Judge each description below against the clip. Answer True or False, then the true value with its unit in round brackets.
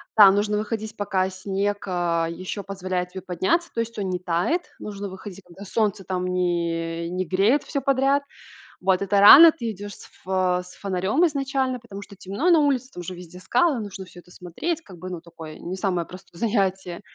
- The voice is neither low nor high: False (195 Hz)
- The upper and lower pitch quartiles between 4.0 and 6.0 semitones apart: False (3.4 semitones)